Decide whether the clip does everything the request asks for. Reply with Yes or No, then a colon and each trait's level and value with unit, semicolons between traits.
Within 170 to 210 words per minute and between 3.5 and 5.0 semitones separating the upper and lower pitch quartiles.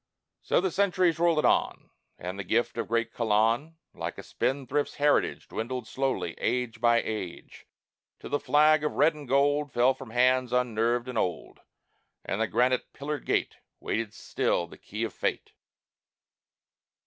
No: average, 155 wpm; average, 4.1 semitones